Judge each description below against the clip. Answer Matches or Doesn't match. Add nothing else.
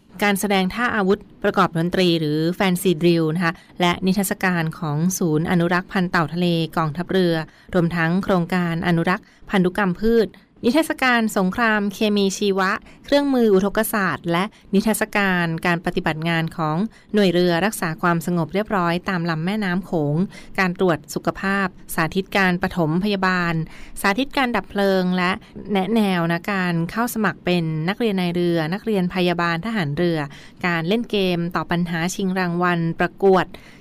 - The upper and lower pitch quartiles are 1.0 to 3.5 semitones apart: Matches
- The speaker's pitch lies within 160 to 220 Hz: Matches